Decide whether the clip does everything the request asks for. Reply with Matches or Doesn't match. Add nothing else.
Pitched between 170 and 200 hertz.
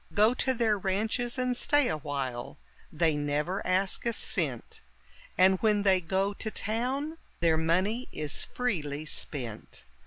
Matches